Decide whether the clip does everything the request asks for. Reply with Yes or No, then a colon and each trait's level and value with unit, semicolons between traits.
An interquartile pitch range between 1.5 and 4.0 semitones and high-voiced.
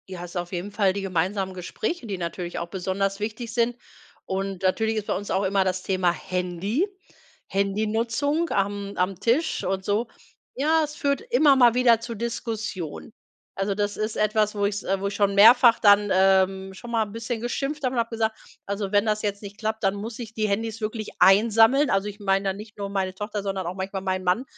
Yes: average, 2.9 semitones; high, 205 Hz